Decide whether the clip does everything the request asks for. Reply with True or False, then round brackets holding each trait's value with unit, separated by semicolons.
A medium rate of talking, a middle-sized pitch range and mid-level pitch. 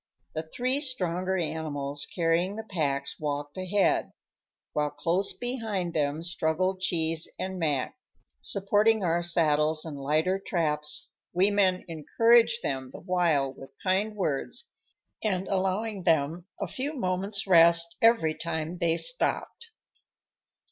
False (125 wpm; 4.1 semitones; 175 Hz)